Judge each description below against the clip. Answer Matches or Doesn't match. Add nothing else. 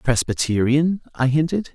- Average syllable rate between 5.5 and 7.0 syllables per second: Doesn't match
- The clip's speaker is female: Doesn't match